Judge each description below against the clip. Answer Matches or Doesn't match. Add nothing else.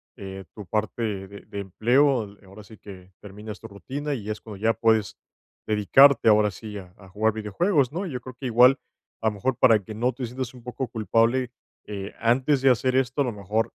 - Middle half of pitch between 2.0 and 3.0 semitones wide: Doesn't match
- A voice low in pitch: Matches